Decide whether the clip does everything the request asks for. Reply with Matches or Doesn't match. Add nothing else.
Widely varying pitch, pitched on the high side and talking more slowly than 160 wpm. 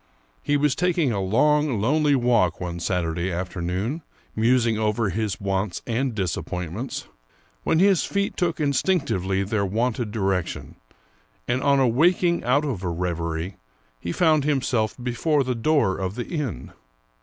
Doesn't match